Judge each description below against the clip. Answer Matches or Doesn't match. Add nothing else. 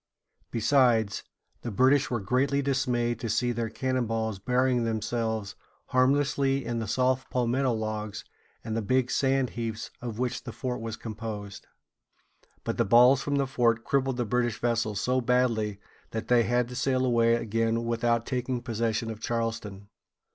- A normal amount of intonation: Doesn't match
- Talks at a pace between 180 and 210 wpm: Doesn't match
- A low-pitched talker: Matches